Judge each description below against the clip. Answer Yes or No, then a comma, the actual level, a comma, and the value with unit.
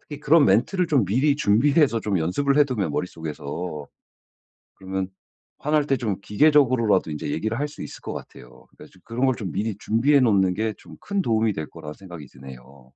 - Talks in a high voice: No, low, 110 Hz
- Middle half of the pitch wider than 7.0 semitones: Yes, wide, 7.5 semitones